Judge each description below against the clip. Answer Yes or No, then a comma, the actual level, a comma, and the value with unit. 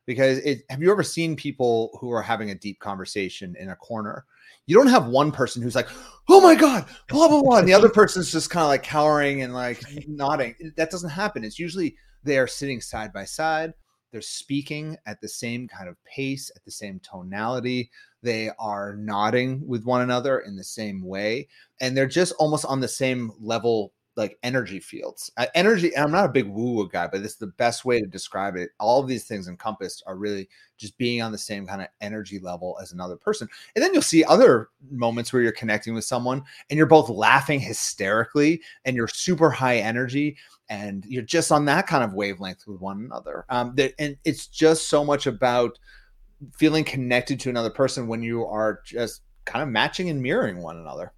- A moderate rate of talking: No, fast, 210 wpm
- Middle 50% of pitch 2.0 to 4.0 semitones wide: No, average, 5.3 semitones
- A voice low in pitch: Yes, low, 125 Hz